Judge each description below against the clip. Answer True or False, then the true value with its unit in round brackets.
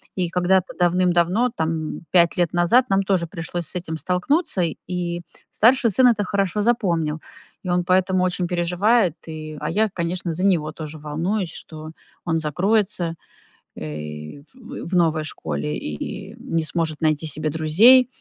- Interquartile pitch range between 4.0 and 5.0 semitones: False (3.3 semitones)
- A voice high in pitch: False (175 Hz)